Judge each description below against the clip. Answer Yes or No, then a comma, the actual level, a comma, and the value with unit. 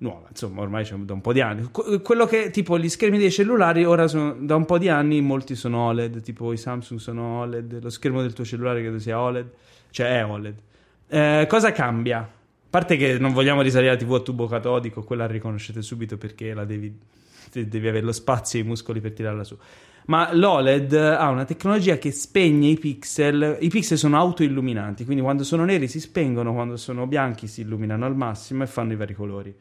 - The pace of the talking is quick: Yes, fast, 215 wpm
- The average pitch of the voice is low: Yes, low, 125 Hz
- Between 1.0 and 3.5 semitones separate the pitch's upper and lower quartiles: No, average, 4.9 semitones